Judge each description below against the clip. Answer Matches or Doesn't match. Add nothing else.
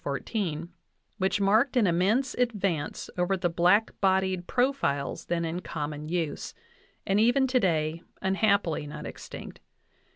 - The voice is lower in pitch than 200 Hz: Matches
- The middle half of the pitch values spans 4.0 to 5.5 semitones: Matches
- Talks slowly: Matches